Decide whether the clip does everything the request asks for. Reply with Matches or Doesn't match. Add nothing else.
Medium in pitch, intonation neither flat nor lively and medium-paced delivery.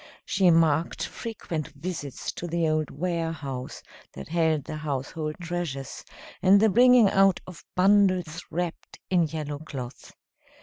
Doesn't match